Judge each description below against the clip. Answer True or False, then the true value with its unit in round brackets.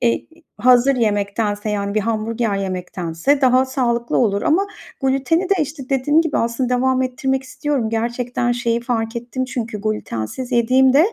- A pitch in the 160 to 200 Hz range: False (240 Hz)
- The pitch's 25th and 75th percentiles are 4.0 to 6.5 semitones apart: False (3.2 semitones)